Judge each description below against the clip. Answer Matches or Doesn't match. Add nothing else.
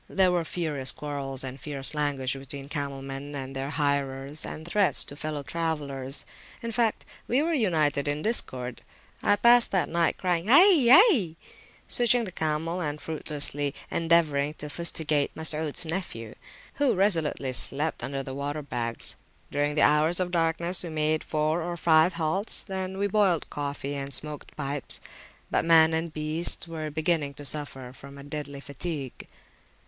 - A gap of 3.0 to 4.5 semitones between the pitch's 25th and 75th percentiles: Matches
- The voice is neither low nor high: Matches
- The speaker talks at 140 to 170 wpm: Matches